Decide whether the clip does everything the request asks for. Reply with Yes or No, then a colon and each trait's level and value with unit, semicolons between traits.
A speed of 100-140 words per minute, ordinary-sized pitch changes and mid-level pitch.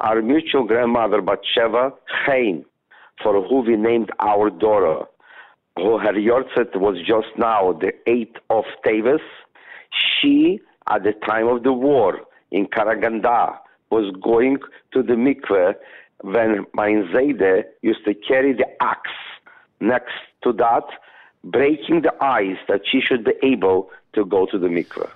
No: slow, 135 wpm; average, 4.2 semitones; low, 115 Hz